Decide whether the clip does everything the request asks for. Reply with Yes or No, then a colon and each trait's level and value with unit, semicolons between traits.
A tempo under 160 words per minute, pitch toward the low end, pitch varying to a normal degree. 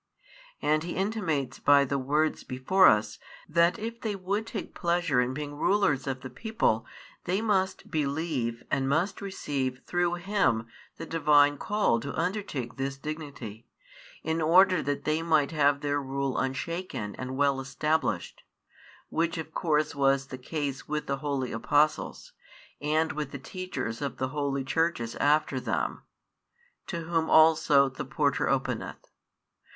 No: average, 145 wpm; medium, 150 Hz; average, 3.9 semitones